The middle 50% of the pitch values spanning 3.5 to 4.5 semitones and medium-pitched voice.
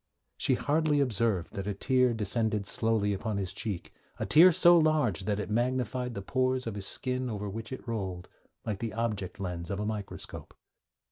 No: average, 4.2 semitones; low, 110 Hz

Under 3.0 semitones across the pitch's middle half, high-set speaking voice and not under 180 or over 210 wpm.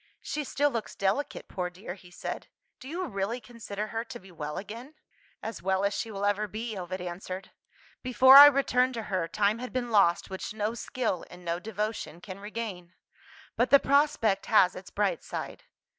No: average, 4.3 semitones; high, 210 Hz; average, 190 wpm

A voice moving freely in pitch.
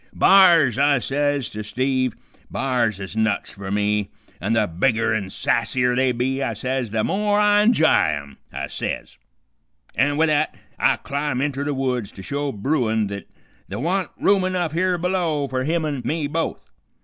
Yes: wide, 5.9 semitones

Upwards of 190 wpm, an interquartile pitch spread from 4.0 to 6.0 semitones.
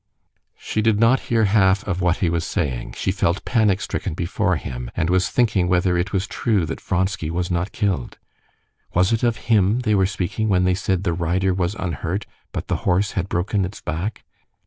No: average, 200 wpm; average, 3.0 semitones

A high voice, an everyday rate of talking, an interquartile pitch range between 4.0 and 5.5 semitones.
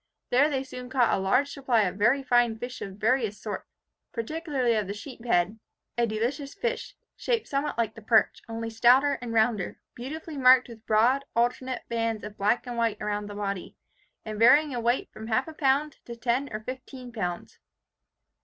No: high, 240 Hz; average, 180 wpm; average, 3.4 semitones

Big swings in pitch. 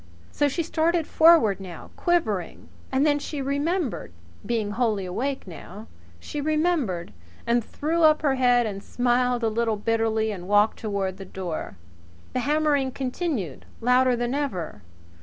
Yes: wide, 6.0 semitones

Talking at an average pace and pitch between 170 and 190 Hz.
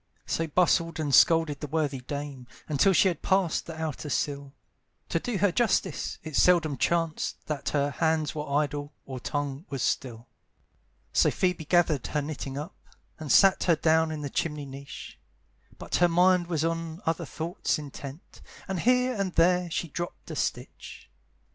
No: average, 165 wpm; medium, 160 Hz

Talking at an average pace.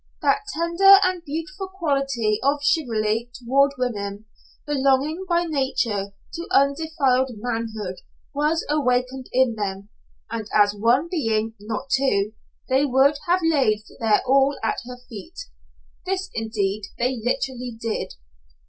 No: slow, 125 wpm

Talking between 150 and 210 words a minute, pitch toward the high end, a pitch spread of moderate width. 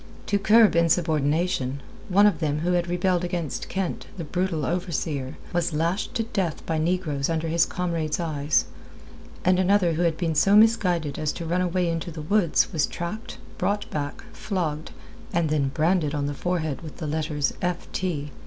No: average, 175 wpm; medium, 170 Hz; average, 3.0 semitones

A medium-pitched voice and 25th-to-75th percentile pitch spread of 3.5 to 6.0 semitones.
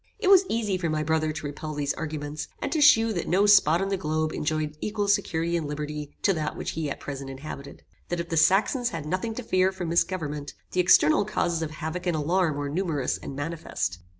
Yes: medium, 160 Hz; average, 4.0 semitones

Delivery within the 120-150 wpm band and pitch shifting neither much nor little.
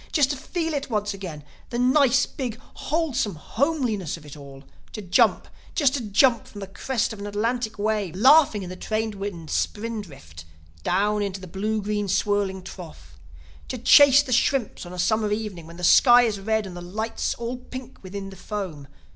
No: average, 190 wpm; average, 4.7 semitones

